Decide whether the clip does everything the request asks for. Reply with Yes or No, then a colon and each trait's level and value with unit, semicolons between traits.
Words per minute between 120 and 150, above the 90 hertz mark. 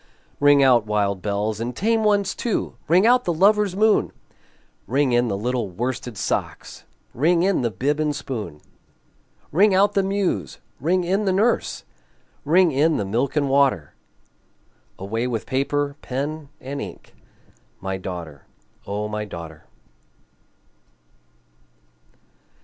Yes: slow, 135 wpm; low, 135 Hz